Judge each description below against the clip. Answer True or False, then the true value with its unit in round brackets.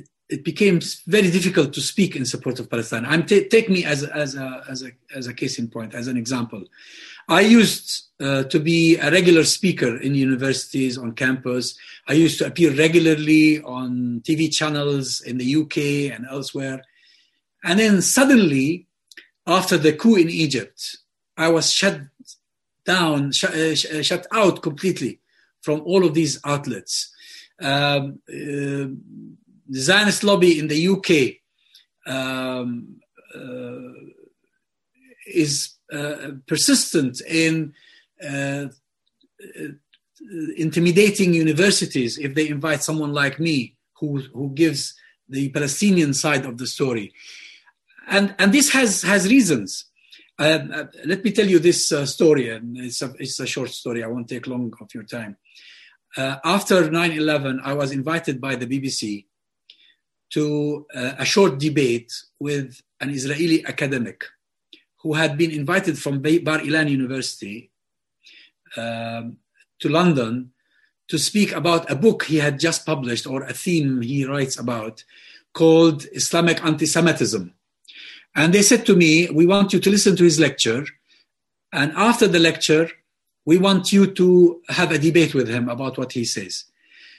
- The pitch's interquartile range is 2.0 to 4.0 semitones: False (4.8 semitones)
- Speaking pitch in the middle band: True (155 Hz)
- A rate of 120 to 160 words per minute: True (145 wpm)